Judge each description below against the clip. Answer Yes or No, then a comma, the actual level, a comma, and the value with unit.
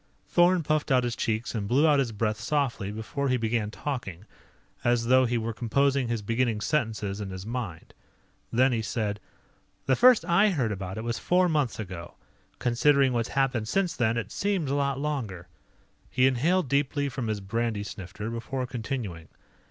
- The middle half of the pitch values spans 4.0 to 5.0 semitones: Yes, average, 4.3 semitones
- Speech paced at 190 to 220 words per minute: No, average, 175 wpm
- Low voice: Yes, low, 120 Hz